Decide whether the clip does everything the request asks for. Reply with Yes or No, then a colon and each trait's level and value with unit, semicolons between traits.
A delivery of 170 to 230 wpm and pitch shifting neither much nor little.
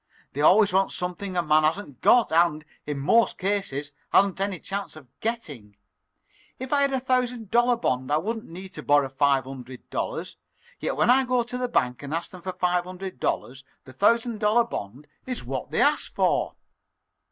No: average, 185 wpm; wide, 7.9 semitones